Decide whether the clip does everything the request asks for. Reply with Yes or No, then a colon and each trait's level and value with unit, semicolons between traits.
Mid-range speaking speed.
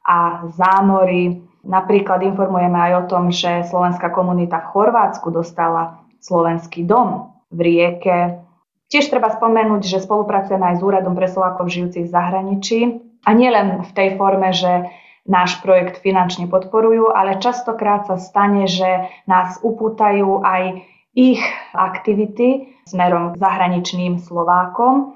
Yes: average, 130 wpm